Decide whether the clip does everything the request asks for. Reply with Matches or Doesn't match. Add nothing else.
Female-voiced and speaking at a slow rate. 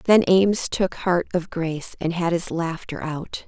Doesn't match